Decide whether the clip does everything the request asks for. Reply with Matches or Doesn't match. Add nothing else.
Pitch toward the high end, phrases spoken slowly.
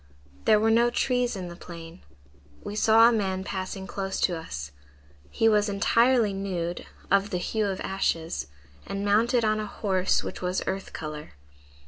Doesn't match